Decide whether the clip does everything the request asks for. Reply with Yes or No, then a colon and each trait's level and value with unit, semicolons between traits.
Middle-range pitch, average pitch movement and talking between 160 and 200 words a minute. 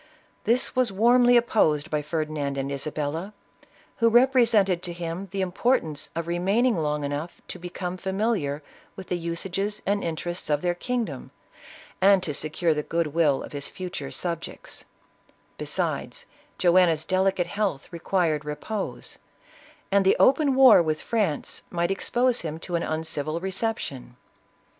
No: medium, 175 Hz; average, 4.8 semitones; average, 145 wpm